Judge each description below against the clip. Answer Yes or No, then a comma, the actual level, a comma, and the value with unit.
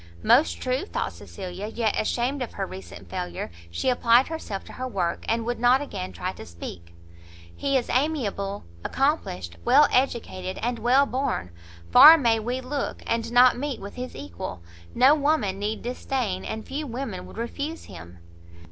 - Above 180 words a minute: No, average, 165 wpm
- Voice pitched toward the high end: Yes, high, 235 Hz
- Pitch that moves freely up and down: Yes, wide, 6.1 semitones